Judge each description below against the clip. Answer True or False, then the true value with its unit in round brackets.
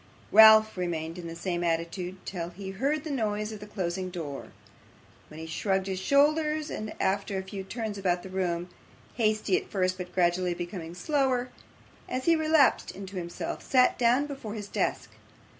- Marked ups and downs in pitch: False (4.6 semitones)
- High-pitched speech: True (195 Hz)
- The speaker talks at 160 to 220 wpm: True (175 wpm)